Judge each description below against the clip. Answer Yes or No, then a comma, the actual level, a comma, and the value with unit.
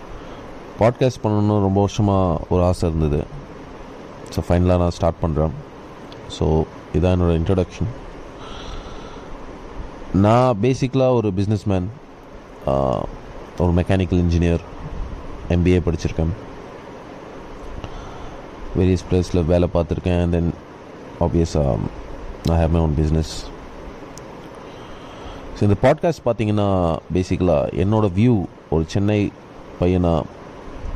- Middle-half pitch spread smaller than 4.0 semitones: Yes, average, 3.3 semitones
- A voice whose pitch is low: Yes, very low, 90 Hz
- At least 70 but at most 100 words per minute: Yes, average, 90 wpm